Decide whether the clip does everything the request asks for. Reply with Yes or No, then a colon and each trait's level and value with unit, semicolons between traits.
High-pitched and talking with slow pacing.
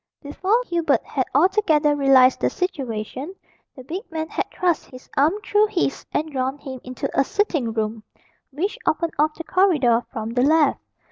No: very high, 295 Hz; average, 165 wpm